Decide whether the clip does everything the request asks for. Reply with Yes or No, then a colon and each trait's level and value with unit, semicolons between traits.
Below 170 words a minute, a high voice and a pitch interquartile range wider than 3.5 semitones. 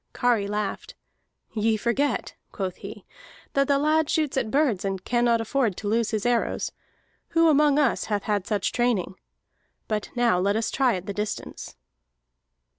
Yes: average, 160 wpm; high, 230 Hz; average, 4.8 semitones